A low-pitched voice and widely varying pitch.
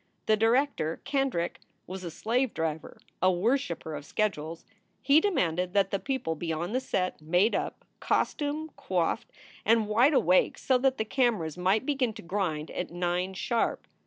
No: high, 195 Hz; wide, 6.9 semitones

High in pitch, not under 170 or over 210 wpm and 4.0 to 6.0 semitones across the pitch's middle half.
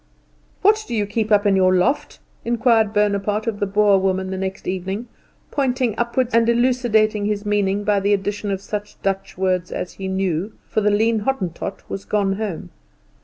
No: high, 205 Hz; average, 180 wpm; narrow, 2.5 semitones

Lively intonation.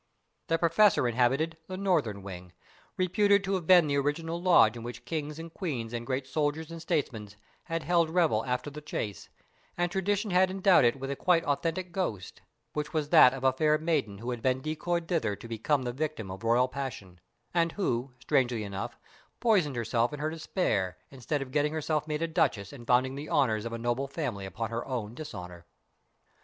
Yes: wide, 5.8 semitones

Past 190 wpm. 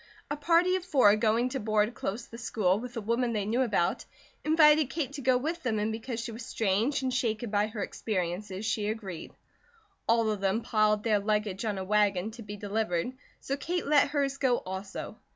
Yes: fast, 205 wpm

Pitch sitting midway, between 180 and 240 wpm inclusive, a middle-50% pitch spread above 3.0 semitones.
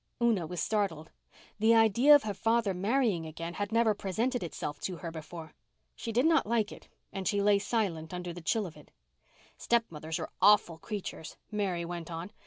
No: high, 200 Hz; average, 185 wpm; average, 4.8 semitones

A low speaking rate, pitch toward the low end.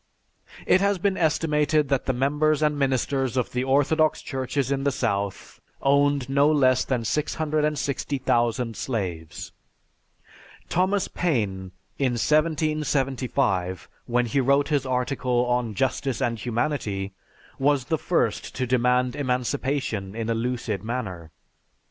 Yes: slow, 125 wpm; low, 130 Hz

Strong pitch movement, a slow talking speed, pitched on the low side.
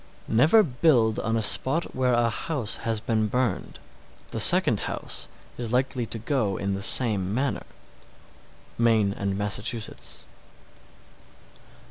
No: average, 3.5 semitones; slow, 130 wpm; low, 115 Hz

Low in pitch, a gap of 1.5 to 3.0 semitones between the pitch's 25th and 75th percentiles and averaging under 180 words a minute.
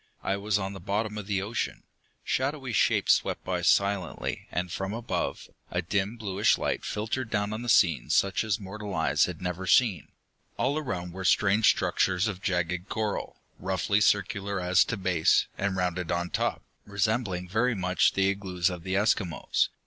Yes: very low, 95 Hz; average, 2.7 semitones; average, 170 wpm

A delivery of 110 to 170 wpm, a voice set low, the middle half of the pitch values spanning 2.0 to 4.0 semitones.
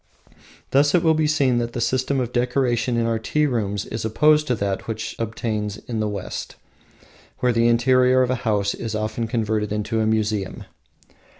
No: average, 185 wpm; low, 115 Hz; average, 2.9 semitones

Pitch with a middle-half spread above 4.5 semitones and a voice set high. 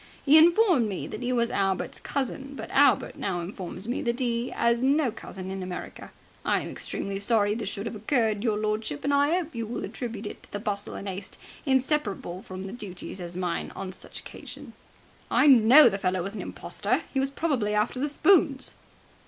Yes: average, 5.3 semitones; high, 225 Hz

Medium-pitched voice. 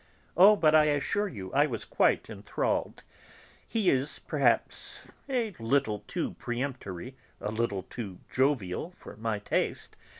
No: low, 130 Hz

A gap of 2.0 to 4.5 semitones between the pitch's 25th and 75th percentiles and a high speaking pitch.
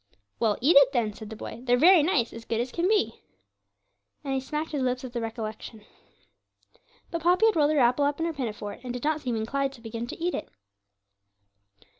No: average, 5.0 semitones; very high, 255 Hz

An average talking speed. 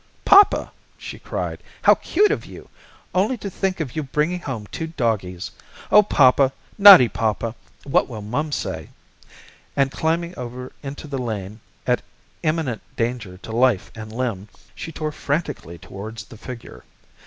Yes: average, 150 wpm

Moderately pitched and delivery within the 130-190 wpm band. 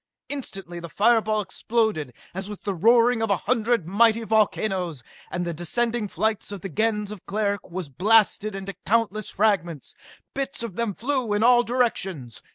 No: high, 210 Hz; average, 165 wpm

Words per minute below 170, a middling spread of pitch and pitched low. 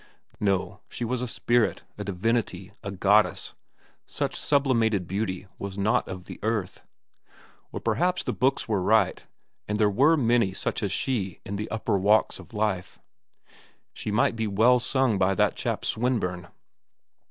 Yes: average, 155 wpm; average, 3.4 semitones; low, 105 Hz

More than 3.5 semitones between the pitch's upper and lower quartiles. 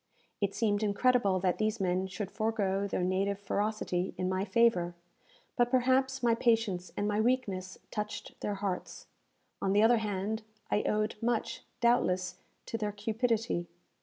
No: average, 3.2 semitones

